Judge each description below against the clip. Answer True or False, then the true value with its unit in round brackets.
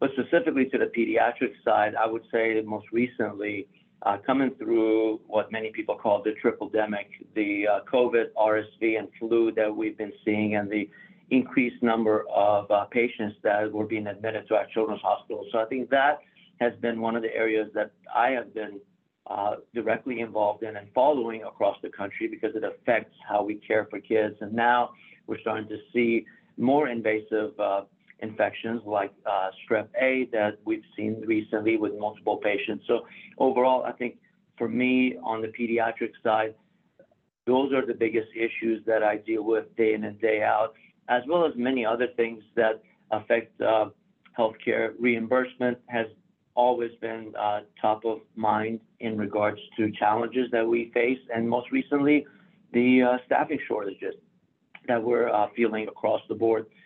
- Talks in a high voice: False (115 Hz)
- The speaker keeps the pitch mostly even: True (2.2 semitones)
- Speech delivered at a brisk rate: False (170 wpm)